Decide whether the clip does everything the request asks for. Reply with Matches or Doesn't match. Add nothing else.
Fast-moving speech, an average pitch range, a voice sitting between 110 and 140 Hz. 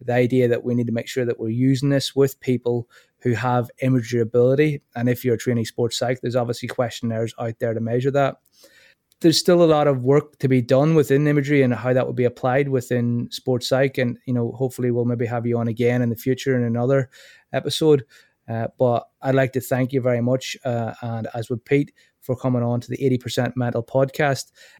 Doesn't match